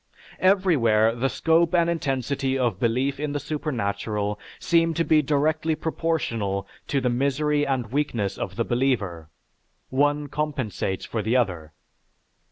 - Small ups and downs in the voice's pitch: No, average, 5.2 semitones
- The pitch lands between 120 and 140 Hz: Yes, low, 135 Hz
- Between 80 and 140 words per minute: Yes, slow, 135 wpm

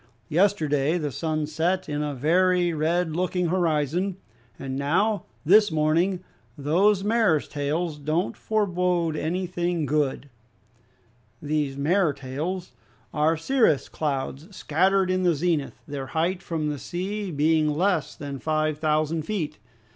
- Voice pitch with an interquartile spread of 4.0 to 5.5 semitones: No, average, 3.4 semitones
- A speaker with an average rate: No, slow, 125 wpm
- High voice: No, medium, 160 Hz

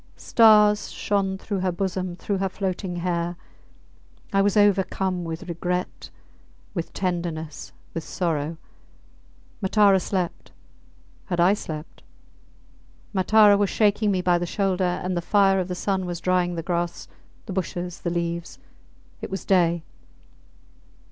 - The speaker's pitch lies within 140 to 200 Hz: Yes, medium, 185 Hz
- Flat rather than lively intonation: Yes, narrow, 2.2 semitones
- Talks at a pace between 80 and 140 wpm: Yes, slow, 135 wpm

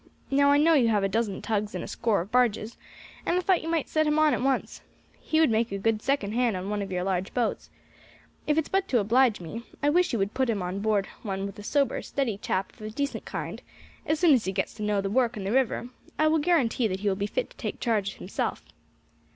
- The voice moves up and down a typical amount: No, wide, 5.9 semitones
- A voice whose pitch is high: Yes, high, 225 Hz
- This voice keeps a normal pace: No, fast, 260 wpm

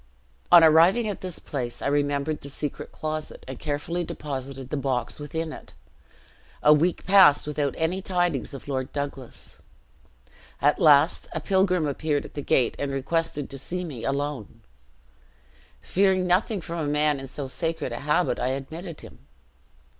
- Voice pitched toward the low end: No, medium, 150 Hz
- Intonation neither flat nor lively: Yes, average, 3.4 semitones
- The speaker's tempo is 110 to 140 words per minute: No, average, 160 wpm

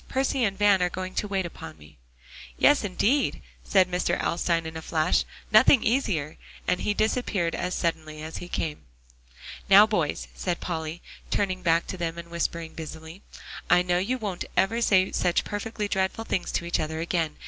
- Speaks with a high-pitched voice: No, medium, 180 Hz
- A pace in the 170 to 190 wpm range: Yes, average, 180 wpm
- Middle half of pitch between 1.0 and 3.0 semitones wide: No, average, 3.8 semitones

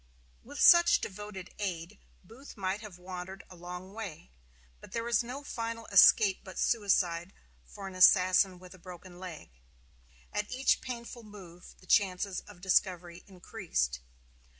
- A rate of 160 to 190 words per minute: No, average, 145 wpm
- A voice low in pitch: No, high, 190 Hz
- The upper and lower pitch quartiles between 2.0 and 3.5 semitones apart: Yes, average, 3.0 semitones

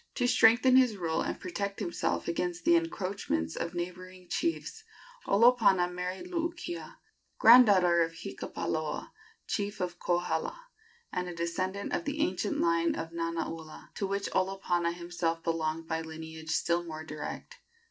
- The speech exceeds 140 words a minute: No, slow, 135 wpm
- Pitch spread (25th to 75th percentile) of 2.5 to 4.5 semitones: Yes, average, 3.4 semitones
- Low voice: No, medium, 180 Hz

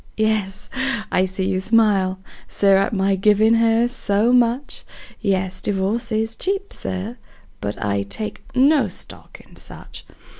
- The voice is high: Yes, high, 210 Hz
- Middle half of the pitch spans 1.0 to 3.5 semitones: Yes, average, 3.2 semitones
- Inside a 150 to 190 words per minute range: No, average, 140 wpm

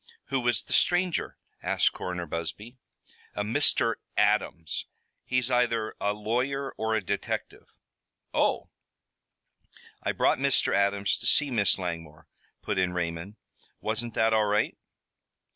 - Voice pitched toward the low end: Yes, low, 105 Hz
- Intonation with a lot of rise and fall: No, average, 4.6 semitones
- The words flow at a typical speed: No, slow, 125 wpm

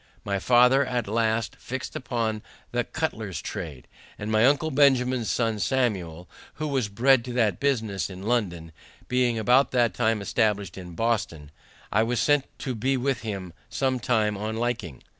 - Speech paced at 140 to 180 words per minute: Yes, average, 160 wpm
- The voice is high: No, low, 115 Hz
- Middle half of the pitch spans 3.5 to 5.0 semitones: Yes, average, 3.8 semitones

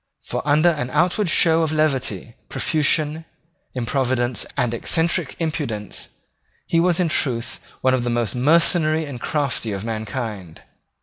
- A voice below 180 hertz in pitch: Yes, low, 135 Hz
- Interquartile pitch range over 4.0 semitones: Yes, average, 5.2 semitones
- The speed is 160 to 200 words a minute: No, slow, 135 wpm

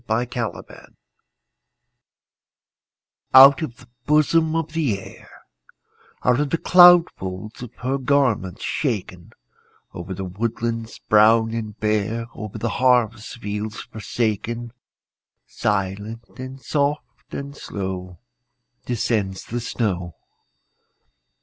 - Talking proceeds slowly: Yes, slow, 105 wpm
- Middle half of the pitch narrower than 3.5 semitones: No, average, 4.2 semitones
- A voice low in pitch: Yes, low, 115 Hz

